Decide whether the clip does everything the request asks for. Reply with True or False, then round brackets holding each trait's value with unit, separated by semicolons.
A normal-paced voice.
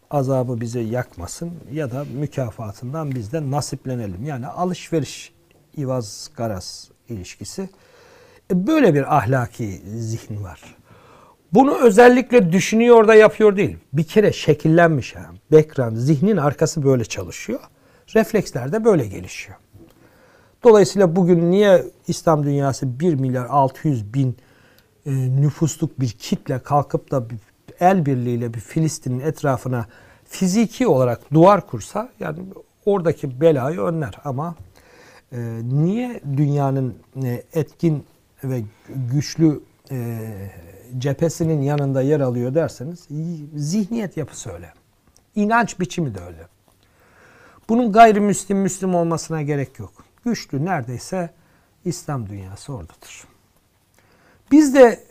True (105 wpm)